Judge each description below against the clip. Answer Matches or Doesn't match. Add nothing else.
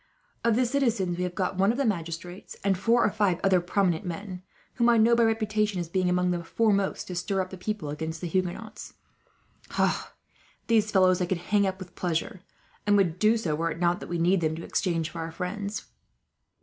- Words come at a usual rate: Doesn't match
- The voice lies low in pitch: Doesn't match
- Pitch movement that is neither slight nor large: Matches